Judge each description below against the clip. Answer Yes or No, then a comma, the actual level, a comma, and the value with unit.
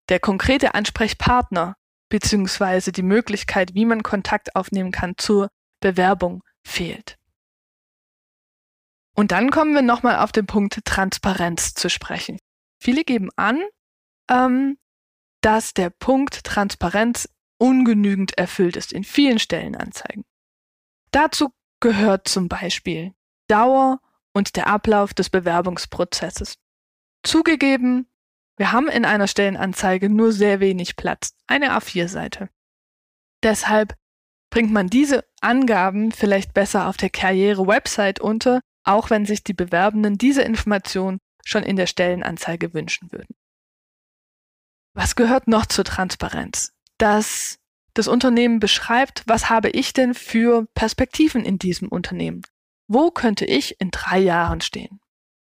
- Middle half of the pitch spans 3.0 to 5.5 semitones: Yes, average, 3.7 semitones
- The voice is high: Yes, high, 210 Hz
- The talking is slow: Yes, slow, 120 wpm